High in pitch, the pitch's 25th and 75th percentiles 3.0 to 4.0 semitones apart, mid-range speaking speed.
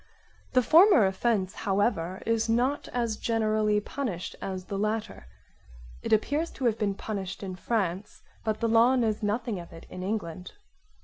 Yes: high, 215 Hz; average, 3.4 semitones; average, 160 wpm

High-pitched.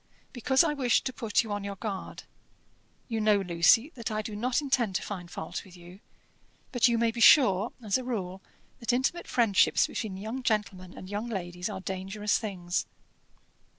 Yes: high, 215 Hz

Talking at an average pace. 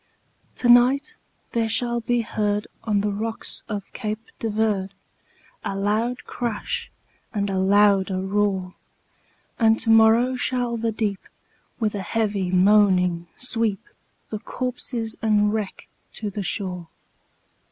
No: slow, 130 wpm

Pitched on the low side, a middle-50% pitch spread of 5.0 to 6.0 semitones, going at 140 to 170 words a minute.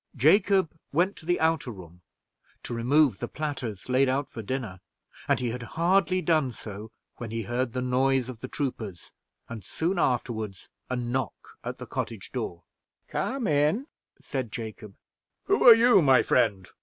Yes: low, 130 Hz; wide, 5.6 semitones; average, 165 wpm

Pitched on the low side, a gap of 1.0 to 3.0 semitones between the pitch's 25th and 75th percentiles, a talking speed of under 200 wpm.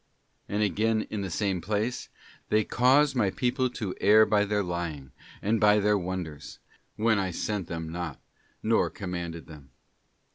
No: low, 100 Hz; average, 3.8 semitones; average, 170 wpm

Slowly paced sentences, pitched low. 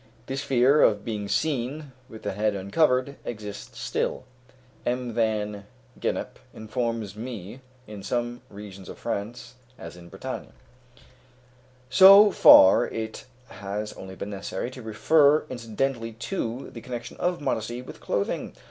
Yes: slow, 130 wpm; low, 115 Hz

